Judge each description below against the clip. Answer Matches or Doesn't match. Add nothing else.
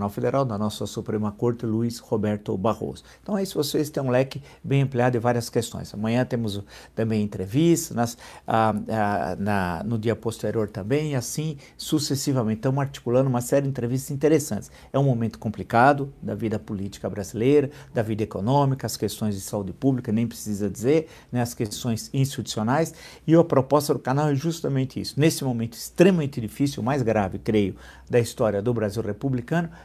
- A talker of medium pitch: Doesn't match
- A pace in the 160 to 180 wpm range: Matches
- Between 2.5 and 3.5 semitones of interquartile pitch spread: Doesn't match